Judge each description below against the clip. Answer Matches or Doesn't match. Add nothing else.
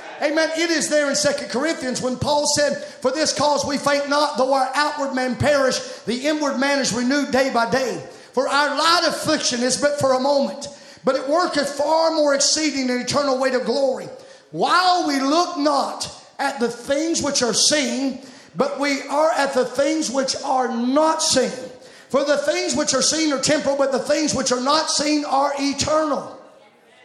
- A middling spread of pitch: Doesn't match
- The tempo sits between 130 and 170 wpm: Doesn't match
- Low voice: Doesn't match